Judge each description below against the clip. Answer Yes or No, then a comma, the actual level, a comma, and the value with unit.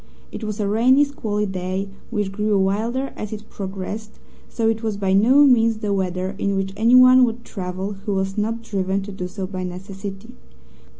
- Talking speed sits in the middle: Yes, average, 185 wpm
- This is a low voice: No, high, 205 Hz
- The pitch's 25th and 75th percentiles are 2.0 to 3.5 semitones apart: Yes, narrow, 2.6 semitones